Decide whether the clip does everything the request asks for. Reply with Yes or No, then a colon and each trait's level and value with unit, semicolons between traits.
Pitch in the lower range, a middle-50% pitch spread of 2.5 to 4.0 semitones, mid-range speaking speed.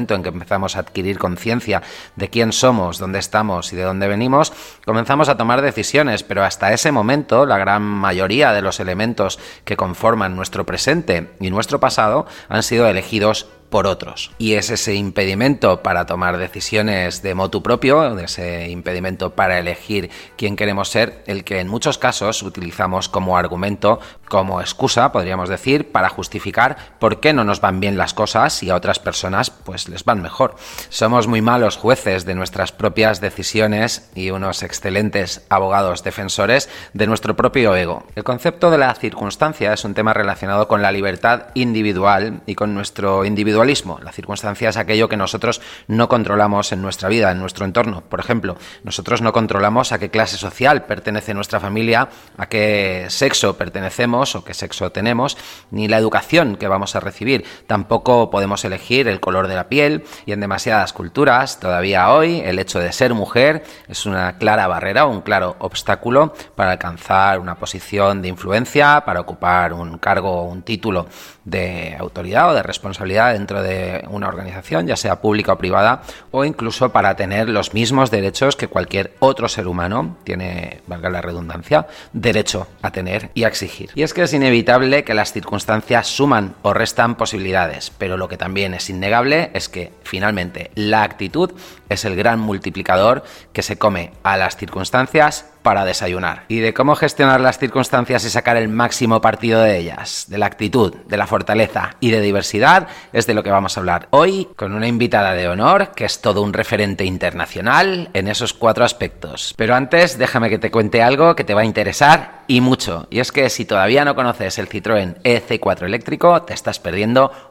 Yes: low, 105 Hz; average, 3.6 semitones; average, 175 wpm